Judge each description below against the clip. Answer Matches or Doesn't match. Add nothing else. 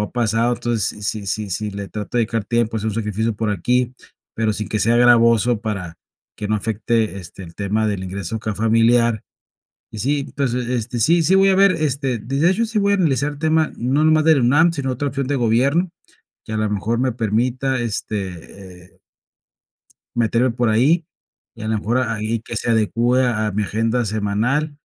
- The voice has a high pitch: Doesn't match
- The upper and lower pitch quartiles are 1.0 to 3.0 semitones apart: Doesn't match